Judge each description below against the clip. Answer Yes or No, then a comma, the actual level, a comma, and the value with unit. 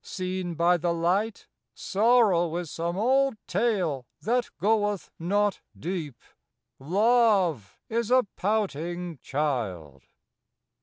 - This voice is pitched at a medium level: Yes, medium, 180 Hz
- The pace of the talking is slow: Yes, slow, 100 wpm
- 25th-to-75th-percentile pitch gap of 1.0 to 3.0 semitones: No, average, 4.6 semitones